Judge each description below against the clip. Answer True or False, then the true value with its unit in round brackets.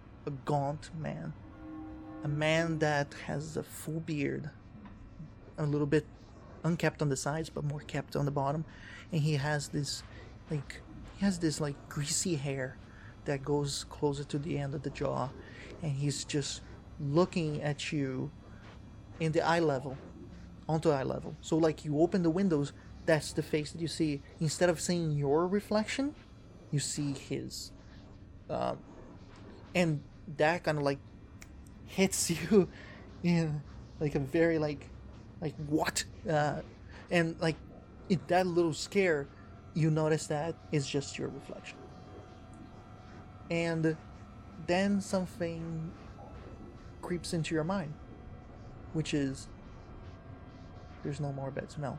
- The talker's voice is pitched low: False (145 Hz)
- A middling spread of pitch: False (7.2 semitones)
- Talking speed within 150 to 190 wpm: False (140 wpm)